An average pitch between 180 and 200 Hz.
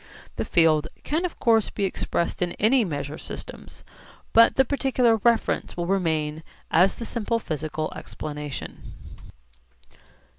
Yes: high, 190 Hz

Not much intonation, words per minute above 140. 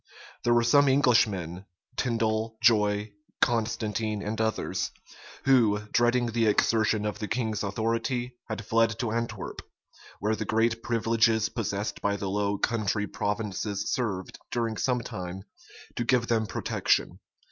No: narrow, 2.1 semitones; slow, 135 wpm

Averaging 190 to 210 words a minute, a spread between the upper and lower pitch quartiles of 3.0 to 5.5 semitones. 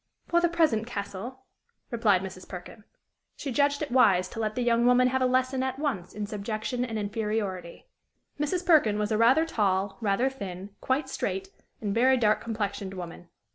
No: average, 175 wpm; average, 4.4 semitones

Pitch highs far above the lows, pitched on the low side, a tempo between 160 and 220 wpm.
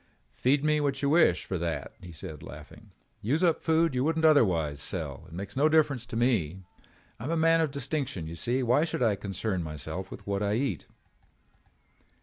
Yes: wide, 8.4 semitones; low, 125 Hz; average, 200 wpm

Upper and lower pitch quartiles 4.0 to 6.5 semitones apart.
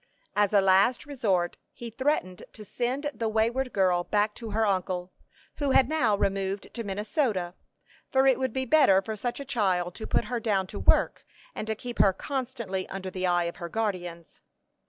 Yes: average, 4.6 semitones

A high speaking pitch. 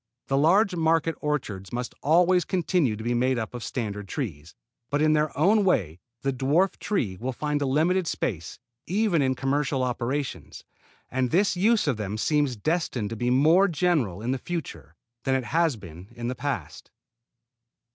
No: low, 135 Hz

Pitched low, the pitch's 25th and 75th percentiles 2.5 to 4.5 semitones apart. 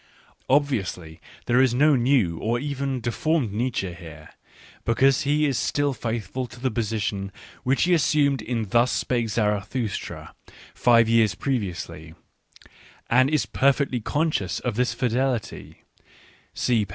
Yes: low, 120 Hz; average, 4.1 semitones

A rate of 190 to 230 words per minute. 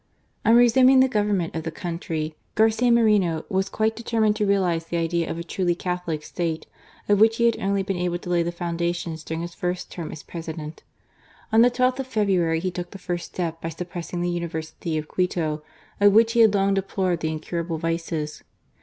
Yes: average, 200 wpm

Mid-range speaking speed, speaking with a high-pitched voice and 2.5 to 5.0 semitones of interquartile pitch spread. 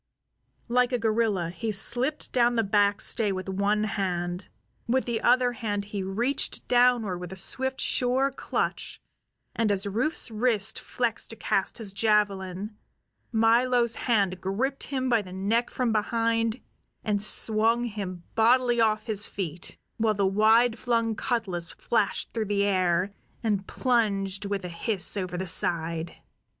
Yes: average, 145 wpm; high, 215 Hz; average, 3.5 semitones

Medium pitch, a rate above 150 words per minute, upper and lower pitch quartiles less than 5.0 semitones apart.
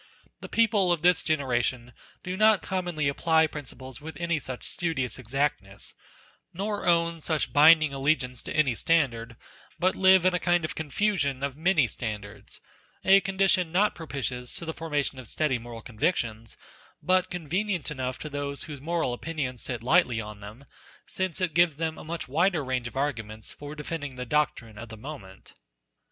No: medium, 150 Hz; average, 170 wpm; average, 5.3 semitones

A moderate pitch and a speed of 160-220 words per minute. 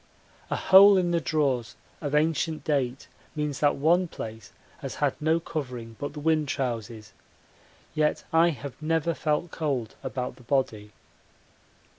No: medium, 145 Hz; average, 145 wpm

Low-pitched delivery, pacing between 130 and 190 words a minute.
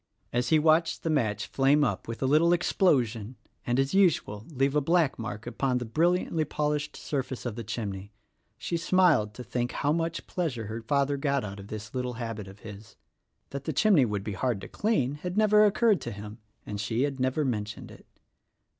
No: low, 130 Hz; average, 200 wpm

